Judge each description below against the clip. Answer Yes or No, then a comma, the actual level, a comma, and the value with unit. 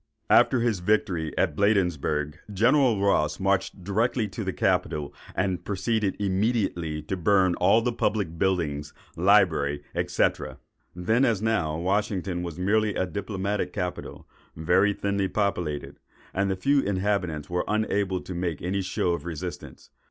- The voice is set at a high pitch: No, very low, 95 Hz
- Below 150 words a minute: Yes, average, 140 wpm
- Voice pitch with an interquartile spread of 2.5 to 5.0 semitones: Yes, average, 3.2 semitones